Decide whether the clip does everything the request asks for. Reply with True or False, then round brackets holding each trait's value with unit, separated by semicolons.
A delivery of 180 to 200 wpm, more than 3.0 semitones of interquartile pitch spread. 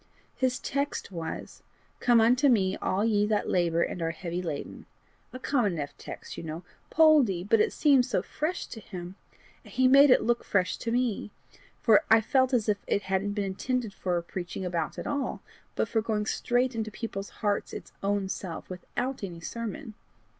True (185 wpm; 5.1 semitones)